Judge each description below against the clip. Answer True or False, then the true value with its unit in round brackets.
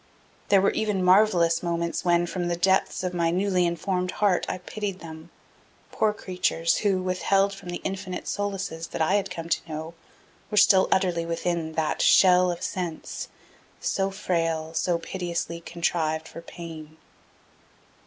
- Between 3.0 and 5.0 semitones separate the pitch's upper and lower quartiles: False (2.4 semitones)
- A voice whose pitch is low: False (175 Hz)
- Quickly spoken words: False (155 wpm)